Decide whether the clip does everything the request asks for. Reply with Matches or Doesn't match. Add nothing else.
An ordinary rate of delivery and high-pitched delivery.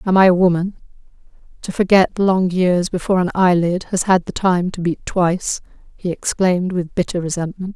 Doesn't match